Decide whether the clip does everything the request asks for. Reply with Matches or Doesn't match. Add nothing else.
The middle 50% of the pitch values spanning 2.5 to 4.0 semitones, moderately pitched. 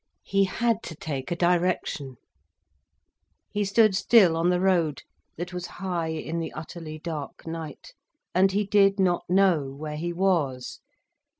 Matches